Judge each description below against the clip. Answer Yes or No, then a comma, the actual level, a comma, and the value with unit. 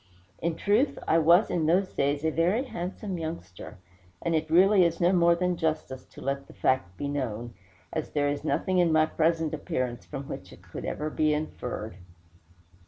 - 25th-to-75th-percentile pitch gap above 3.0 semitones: Yes, average, 3.4 semitones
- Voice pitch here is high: No, medium, 160 Hz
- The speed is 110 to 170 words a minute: No, average, 185 wpm